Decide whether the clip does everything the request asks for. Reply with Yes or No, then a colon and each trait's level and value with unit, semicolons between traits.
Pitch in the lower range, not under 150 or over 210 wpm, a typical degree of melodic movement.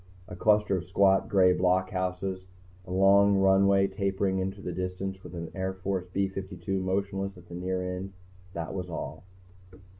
No: very low, 95 Hz; average, 160 wpm; narrow, 1.1 semitones